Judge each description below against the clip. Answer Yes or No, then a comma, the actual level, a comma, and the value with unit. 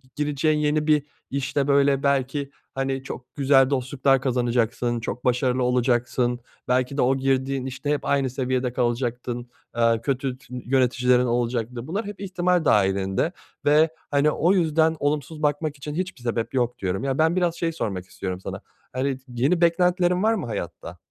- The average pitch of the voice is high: No, low, 135 Hz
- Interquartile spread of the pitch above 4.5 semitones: No, average, 3.4 semitones